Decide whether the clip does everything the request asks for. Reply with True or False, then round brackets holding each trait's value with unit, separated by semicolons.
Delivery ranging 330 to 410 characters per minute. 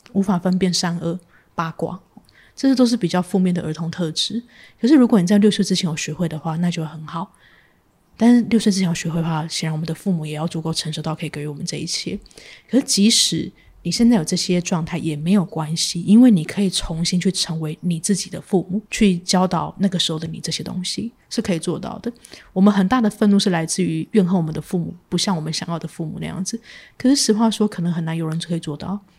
True (355 characters per minute)